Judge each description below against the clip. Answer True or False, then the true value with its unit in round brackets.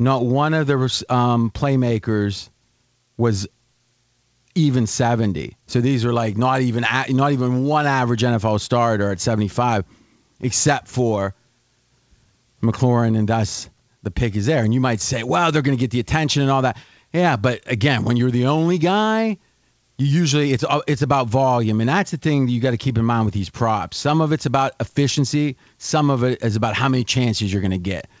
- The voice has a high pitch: False (125 Hz)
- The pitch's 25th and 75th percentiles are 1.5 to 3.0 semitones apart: False (3.5 semitones)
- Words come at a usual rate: True (195 wpm)